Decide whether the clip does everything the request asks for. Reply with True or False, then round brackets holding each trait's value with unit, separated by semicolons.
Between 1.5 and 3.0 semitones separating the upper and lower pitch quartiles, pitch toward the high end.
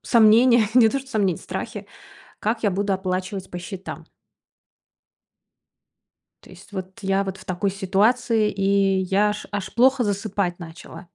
True (2.5 semitones; 200 Hz)